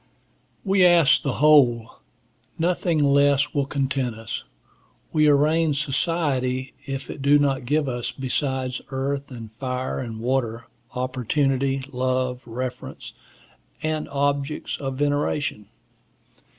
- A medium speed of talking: No, slow, 110 wpm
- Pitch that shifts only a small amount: Yes, narrow, 2.3 semitones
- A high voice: No, low, 135 Hz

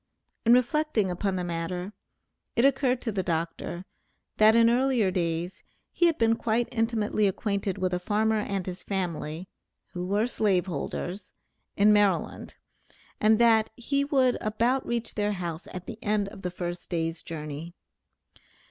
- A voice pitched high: Yes, high, 205 Hz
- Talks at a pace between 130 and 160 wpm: Yes, average, 155 wpm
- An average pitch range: Yes, average, 4.3 semitones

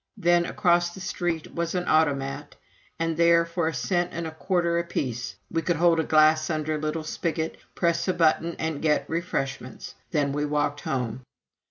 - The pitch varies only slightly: Yes, narrow, 2.2 semitones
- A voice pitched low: No, medium, 160 Hz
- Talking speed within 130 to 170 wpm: No, average, 180 wpm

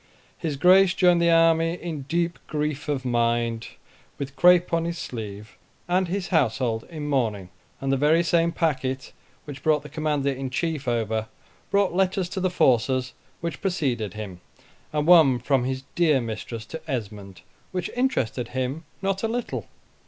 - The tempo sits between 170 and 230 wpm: No, average, 160 wpm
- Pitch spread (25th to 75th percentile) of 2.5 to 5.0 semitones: No, wide, 5.6 semitones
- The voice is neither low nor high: Yes, medium, 150 Hz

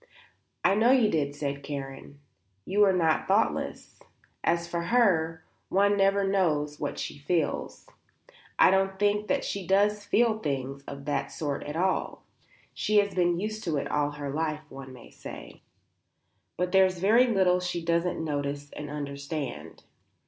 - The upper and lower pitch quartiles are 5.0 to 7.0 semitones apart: Yes, average, 5.3 semitones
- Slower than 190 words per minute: Yes, average, 155 wpm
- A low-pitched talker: No, medium, 170 Hz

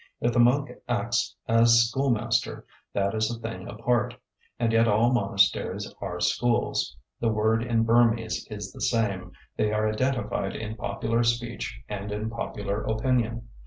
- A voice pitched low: Yes, low, 115 Hz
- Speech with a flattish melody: Yes, narrow, 1.9 semitones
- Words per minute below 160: Yes, average, 150 wpm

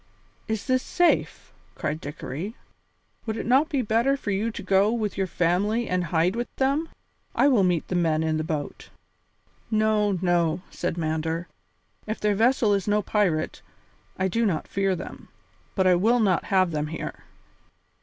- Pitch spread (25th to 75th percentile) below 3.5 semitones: No, average, 4.6 semitones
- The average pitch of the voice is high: Yes, high, 195 Hz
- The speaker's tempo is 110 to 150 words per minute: No, average, 170 wpm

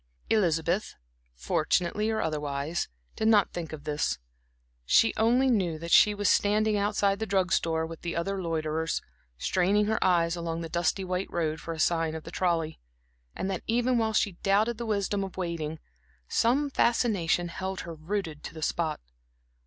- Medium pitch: Yes, medium, 175 Hz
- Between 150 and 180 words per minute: Yes, average, 170 wpm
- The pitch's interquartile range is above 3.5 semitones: Yes, average, 4.3 semitones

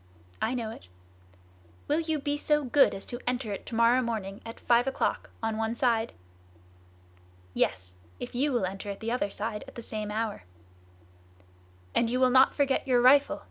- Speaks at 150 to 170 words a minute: No, average, 180 wpm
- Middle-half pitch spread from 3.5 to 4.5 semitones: No, average, 3.1 semitones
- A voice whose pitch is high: Yes, high, 235 Hz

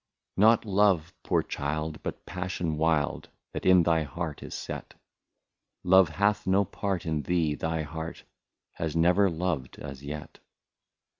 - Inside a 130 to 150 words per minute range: Yes, average, 140 wpm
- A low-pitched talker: Yes, very low, 85 Hz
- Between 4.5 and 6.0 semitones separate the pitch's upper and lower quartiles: No, average, 3.3 semitones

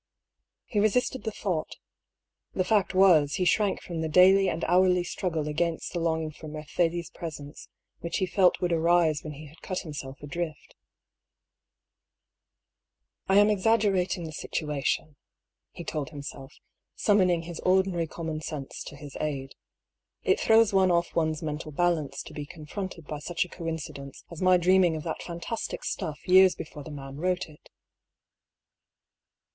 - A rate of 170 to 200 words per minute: No, average, 155 wpm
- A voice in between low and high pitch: Yes, medium, 170 Hz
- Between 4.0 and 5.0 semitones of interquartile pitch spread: No, average, 3.2 semitones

